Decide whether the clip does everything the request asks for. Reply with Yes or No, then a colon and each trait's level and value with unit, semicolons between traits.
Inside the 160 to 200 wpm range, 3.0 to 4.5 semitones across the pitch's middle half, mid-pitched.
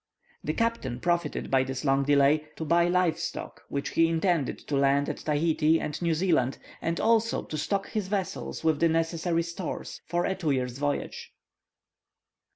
Yes: average, 170 wpm; average, 3.4 semitones; medium, 160 Hz